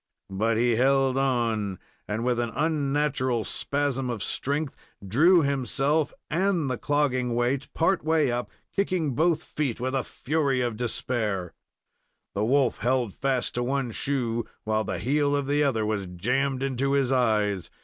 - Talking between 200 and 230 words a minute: No, average, 155 wpm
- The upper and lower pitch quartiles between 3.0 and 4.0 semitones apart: Yes, average, 3.4 semitones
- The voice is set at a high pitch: No, low, 130 Hz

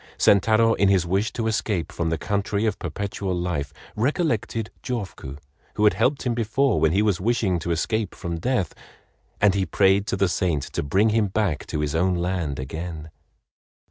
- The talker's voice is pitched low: Yes, very low, 95 Hz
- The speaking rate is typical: Yes, average, 175 wpm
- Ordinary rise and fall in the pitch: Yes, average, 4.4 semitones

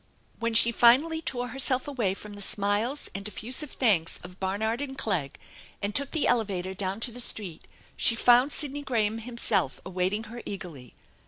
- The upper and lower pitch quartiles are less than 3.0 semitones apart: No, average, 4.2 semitones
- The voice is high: Yes, high, 220 Hz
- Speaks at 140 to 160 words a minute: No, average, 170 wpm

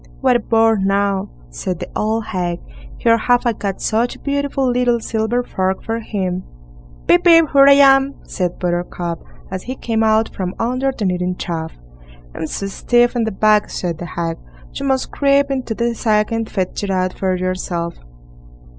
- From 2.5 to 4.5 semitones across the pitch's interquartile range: No, average, 4.9 semitones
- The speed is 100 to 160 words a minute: No, average, 180 wpm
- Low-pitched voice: No, high, 220 Hz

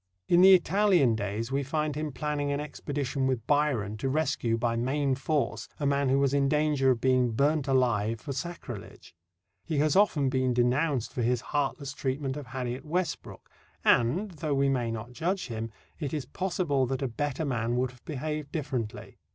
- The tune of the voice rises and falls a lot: No, average, 3.3 semitones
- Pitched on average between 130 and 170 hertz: Yes, low, 135 Hz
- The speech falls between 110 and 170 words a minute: No, average, 185 wpm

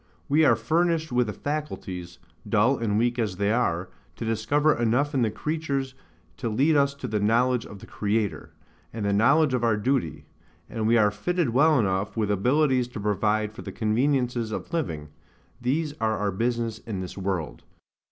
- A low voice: Yes, low, 115 Hz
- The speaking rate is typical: Yes, average, 180 wpm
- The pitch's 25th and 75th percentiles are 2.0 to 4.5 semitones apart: No, average, 4.9 semitones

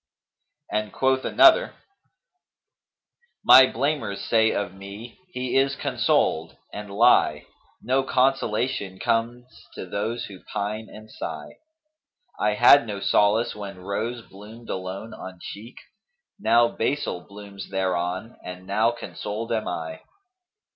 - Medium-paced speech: No, slow, 125 wpm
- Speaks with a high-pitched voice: No, low, 110 Hz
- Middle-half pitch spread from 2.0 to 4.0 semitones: Yes, average, 3.5 semitones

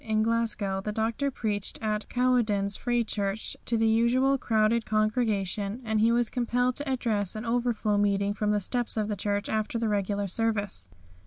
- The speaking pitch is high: Yes, high, 220 Hz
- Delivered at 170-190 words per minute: Yes, average, 180 wpm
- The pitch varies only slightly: Yes, narrow, 2.3 semitones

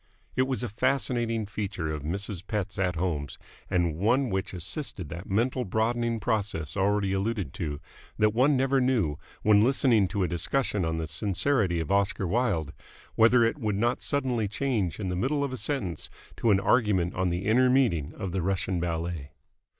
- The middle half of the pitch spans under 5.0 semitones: No, wide, 5.4 semitones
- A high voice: No, low, 100 Hz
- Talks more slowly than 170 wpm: No, average, 180 wpm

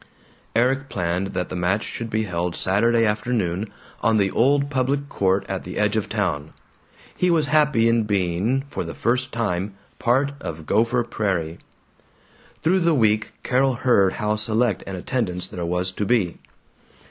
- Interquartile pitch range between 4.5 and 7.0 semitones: Yes, average, 5.1 semitones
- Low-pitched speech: Yes, low, 110 Hz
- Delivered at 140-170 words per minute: Yes, average, 160 wpm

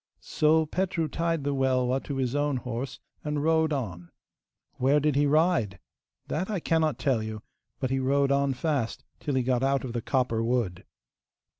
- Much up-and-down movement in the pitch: No, average, 3.4 semitones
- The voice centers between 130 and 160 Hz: Yes, low, 135 Hz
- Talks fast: No, average, 175 wpm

